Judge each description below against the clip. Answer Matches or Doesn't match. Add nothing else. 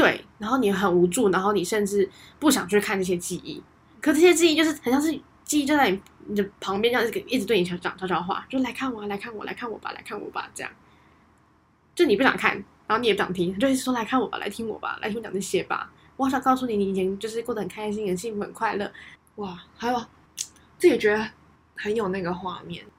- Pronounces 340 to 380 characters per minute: Matches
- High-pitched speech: Matches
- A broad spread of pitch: Doesn't match